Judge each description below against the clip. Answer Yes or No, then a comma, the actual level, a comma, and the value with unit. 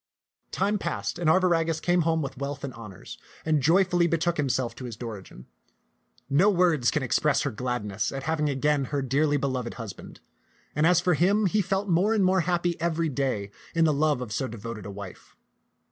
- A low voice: No, medium, 150 Hz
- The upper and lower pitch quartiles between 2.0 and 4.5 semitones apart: No, wide, 5.5 semitones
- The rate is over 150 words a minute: Yes, average, 190 wpm